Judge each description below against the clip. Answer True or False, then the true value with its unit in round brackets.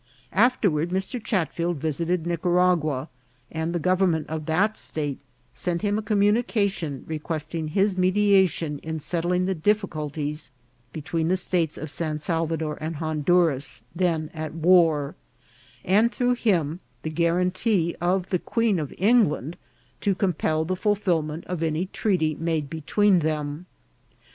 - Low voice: False (170 Hz)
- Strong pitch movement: False (3.3 semitones)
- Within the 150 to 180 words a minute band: False (135 wpm)